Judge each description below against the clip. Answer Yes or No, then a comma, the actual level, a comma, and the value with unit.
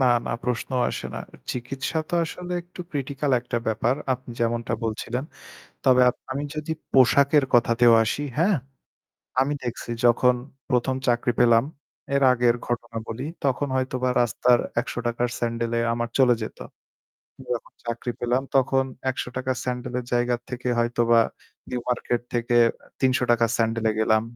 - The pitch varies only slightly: Yes, narrow, 1.8 semitones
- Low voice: Yes, low, 125 Hz